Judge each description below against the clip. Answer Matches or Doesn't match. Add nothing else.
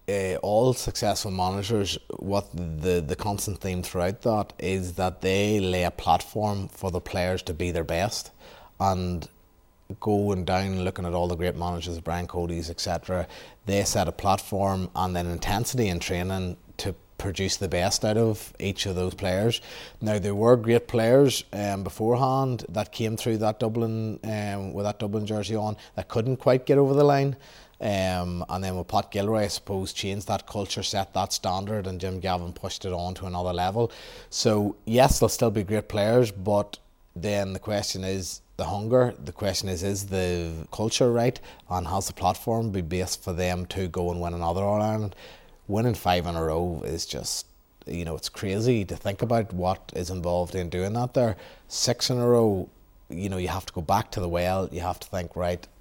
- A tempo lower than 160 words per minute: Doesn't match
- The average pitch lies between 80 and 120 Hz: Matches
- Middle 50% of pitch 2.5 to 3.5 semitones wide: Matches